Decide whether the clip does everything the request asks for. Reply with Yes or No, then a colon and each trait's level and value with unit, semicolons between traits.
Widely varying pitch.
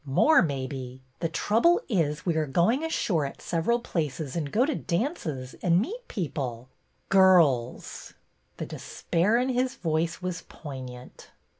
Yes: wide, 8.1 semitones